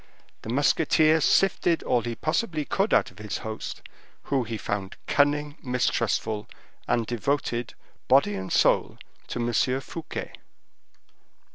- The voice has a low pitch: Yes, low, 125 Hz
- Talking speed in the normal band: No, slow, 125 wpm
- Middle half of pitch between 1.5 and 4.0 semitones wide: No, average, 4.9 semitones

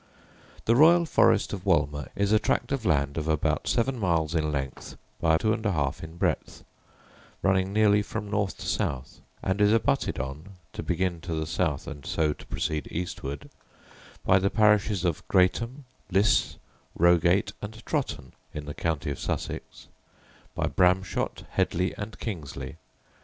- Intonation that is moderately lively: Yes, average, 5.0 semitones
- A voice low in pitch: Yes, very low, 90 Hz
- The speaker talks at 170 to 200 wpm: No, average, 160 wpm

